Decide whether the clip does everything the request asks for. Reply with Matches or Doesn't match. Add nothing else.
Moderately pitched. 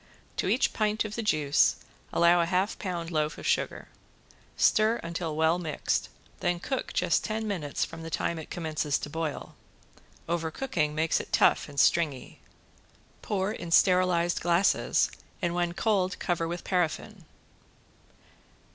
Matches